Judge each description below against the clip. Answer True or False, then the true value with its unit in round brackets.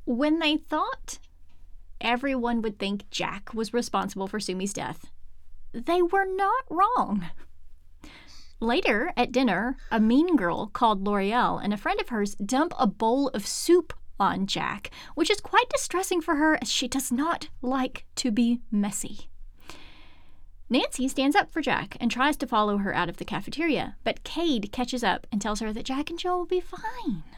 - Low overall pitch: False (240 Hz)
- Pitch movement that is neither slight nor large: False (7.7 semitones)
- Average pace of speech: True (170 wpm)